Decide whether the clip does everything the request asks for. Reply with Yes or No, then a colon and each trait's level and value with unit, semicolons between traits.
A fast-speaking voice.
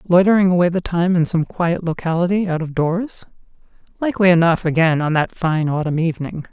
No: average, 175 wpm